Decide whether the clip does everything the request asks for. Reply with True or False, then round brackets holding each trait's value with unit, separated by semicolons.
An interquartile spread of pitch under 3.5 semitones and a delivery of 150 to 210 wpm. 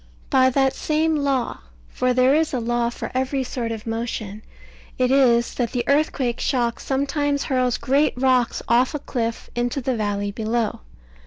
True (2.6 semitones; 165 wpm)